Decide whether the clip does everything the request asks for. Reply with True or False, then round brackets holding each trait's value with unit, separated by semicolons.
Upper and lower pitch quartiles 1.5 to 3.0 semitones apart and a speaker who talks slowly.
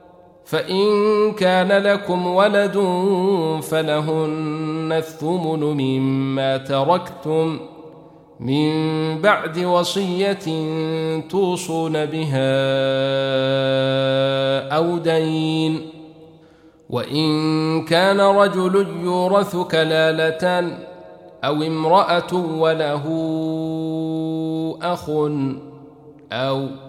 True (2.7 semitones; 55 wpm)